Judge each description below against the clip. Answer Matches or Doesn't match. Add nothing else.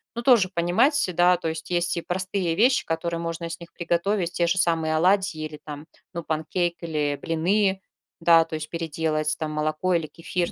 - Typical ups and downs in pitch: Doesn't match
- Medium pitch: Matches